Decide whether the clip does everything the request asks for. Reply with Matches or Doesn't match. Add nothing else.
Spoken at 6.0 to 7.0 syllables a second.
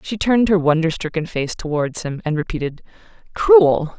Doesn't match